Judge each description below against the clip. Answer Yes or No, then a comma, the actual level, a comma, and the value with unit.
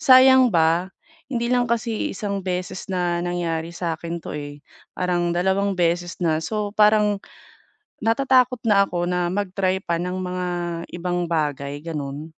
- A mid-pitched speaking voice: Yes, medium, 180 Hz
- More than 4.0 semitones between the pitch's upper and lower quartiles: No, average, 3.5 semitones